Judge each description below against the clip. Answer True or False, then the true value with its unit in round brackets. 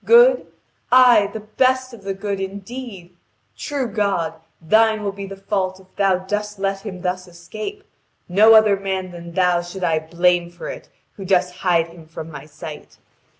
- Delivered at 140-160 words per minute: False (175 wpm)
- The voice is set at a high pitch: True (195 Hz)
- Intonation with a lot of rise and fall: False (3.2 semitones)